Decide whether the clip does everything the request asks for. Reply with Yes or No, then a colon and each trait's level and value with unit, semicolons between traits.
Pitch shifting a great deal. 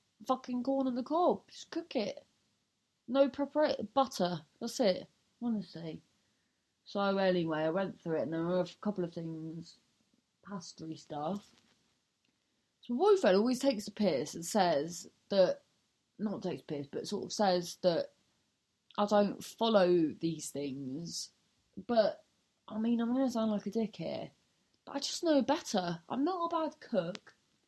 Yes: wide, 6.7 semitones